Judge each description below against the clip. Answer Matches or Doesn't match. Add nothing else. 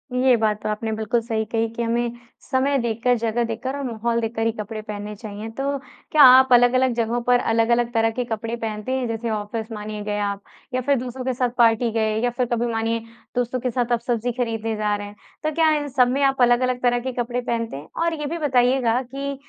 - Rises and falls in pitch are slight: Matches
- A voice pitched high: Matches